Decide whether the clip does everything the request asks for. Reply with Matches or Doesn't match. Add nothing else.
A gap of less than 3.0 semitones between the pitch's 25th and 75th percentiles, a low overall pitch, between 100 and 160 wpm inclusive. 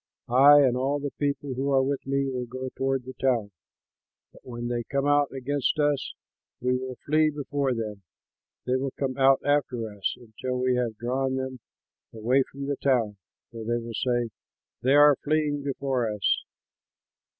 Doesn't match